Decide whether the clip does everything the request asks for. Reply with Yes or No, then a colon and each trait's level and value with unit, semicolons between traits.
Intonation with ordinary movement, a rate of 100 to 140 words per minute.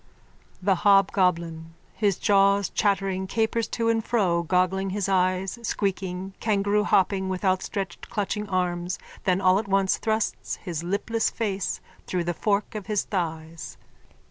No: narrow, 2.1 semitones; slow, 135 wpm